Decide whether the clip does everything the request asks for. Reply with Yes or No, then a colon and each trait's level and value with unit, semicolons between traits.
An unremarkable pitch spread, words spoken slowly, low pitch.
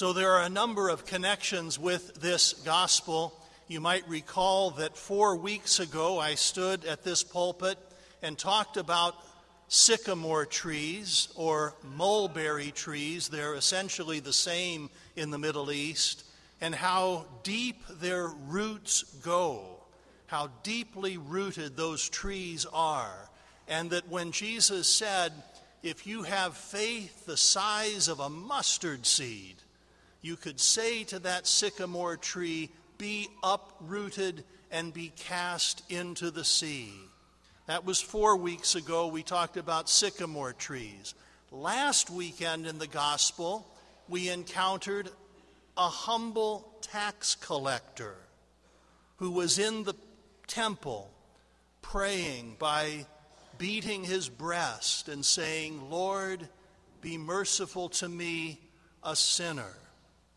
No: average, 3.3 semitones; slow, 120 wpm; medium, 175 Hz